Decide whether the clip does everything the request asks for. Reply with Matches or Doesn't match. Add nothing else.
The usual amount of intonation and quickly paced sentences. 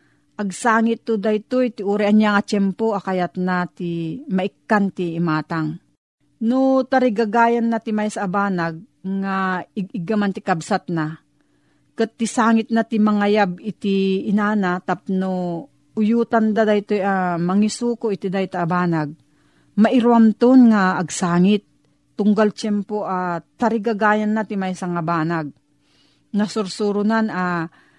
Doesn't match